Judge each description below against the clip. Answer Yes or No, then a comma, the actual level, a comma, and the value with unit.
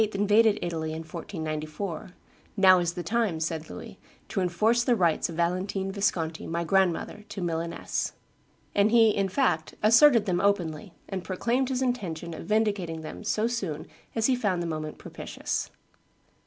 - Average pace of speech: Yes, average, 155 wpm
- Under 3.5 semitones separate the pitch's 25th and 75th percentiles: No, average, 4.5 semitones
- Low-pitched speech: No, medium, 185 Hz